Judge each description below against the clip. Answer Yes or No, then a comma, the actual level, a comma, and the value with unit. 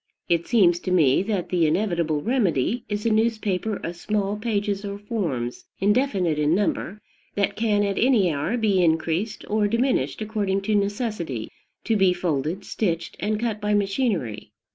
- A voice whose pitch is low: No, high, 200 Hz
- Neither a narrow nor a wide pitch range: Yes, average, 3.9 semitones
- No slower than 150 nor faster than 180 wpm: Yes, average, 160 wpm